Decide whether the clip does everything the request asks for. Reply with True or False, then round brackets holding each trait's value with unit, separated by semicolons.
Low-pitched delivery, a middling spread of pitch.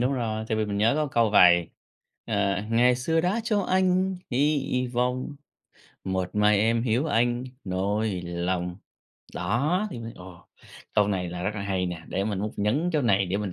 True (110 Hz; 5.0 semitones)